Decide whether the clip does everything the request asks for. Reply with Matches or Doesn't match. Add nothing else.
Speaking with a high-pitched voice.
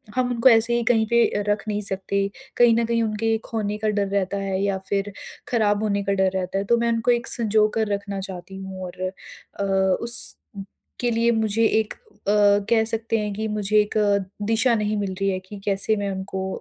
Matches